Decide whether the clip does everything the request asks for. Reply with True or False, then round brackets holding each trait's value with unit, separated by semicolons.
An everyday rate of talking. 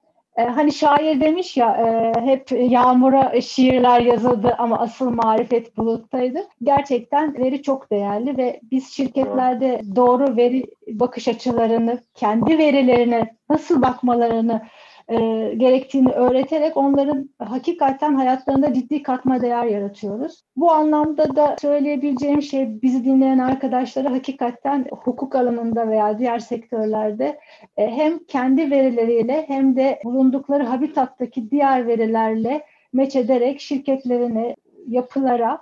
True (105 wpm)